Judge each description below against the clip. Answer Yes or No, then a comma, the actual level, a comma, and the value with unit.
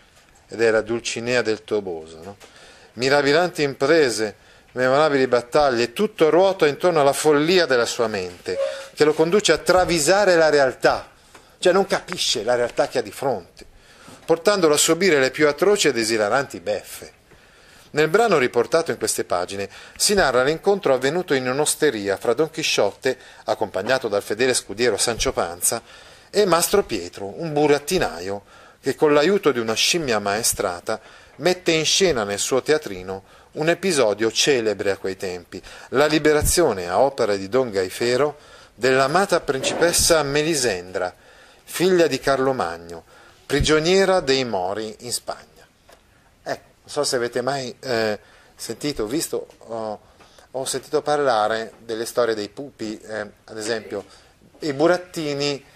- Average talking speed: Yes, average, 140 wpm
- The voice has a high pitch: No, medium, 140 Hz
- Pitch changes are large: Yes, wide, 6.6 semitones